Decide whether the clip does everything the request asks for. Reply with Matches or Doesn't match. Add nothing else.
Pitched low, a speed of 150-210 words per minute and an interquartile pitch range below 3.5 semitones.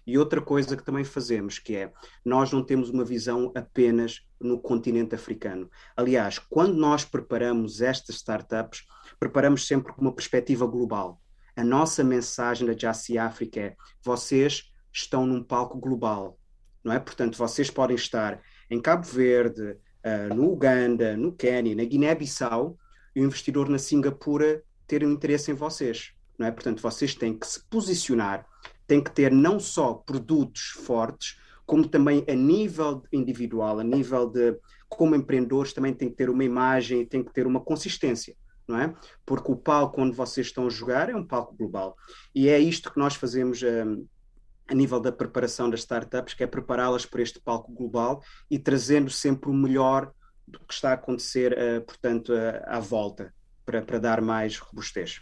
Matches